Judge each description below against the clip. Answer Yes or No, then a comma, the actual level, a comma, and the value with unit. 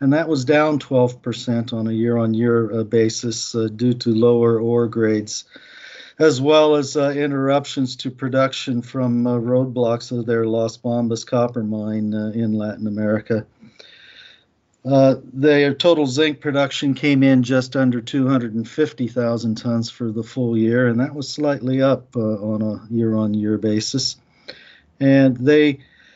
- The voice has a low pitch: Yes, low, 120 Hz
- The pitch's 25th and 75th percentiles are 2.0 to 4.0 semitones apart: Yes, average, 3.0 semitones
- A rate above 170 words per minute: No, average, 140 wpm